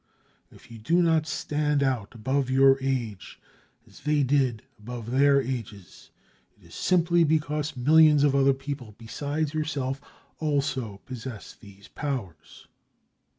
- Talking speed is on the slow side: Yes, slow, 130 wpm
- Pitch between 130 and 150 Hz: Yes, low, 135 Hz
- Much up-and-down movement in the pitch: No, average, 3.6 semitones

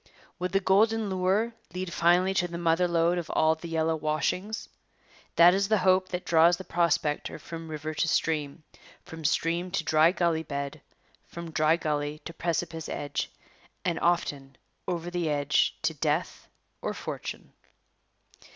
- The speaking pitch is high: No, medium, 170 Hz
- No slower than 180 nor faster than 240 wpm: No, average, 155 wpm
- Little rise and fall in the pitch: Yes, narrow, 2.3 semitones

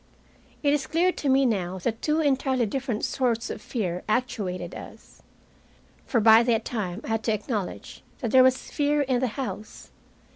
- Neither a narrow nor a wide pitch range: Yes, average, 3.8 semitones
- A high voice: Yes, high, 240 Hz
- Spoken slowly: No, average, 175 wpm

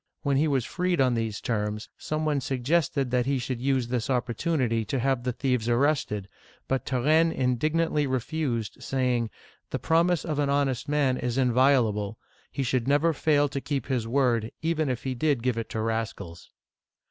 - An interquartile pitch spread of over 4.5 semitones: No, average, 3.5 semitones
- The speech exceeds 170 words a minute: Yes, average, 185 wpm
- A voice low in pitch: Yes, low, 130 Hz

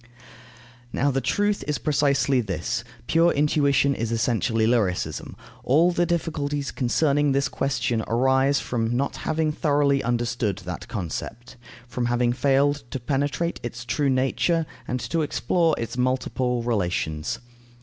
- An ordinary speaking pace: No, slow, 130 wpm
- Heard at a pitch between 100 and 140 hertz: Yes, low, 135 Hz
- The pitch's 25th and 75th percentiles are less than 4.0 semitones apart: Yes, average, 3.4 semitones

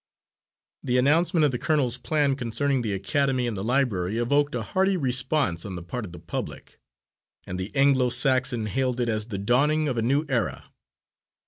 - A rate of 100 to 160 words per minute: No, average, 185 wpm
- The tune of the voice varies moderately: Yes, average, 4.2 semitones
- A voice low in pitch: Yes, low, 125 Hz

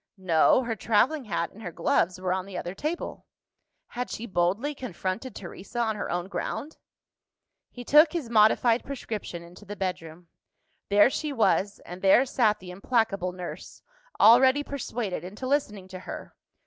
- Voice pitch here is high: Yes, high, 210 Hz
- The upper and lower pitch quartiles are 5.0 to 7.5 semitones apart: Yes, average, 5.3 semitones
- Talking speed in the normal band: Yes, average, 160 wpm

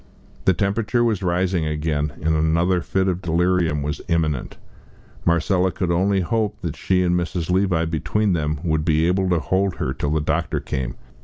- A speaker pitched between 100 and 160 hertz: No, very low, 85 Hz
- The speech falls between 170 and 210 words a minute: Yes, average, 175 wpm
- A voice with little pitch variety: No, average, 3.1 semitones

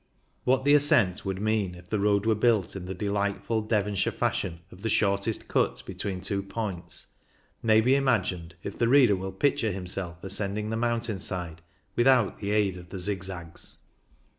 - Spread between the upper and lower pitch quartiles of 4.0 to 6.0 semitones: No, average, 3.2 semitones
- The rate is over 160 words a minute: Yes, average, 170 wpm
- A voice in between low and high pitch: No, low, 100 Hz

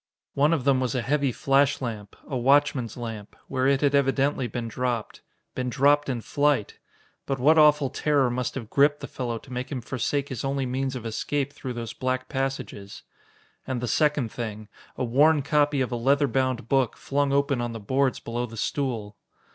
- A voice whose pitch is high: No, low, 130 Hz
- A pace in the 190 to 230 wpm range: Yes, average, 195 wpm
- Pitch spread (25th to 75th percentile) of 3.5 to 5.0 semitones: No, average, 2.8 semitones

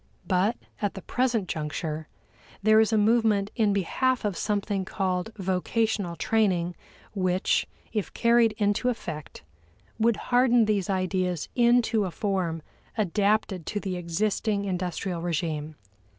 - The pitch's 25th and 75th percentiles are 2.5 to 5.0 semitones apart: Yes, average, 3.5 semitones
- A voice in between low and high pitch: No, high, 200 Hz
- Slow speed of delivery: Yes, slow, 125 wpm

